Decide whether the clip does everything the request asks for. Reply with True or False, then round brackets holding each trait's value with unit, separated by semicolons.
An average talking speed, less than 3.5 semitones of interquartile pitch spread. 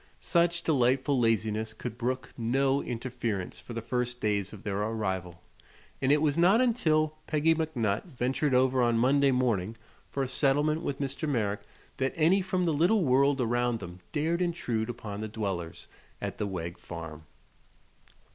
False (160 wpm; 5.5 semitones)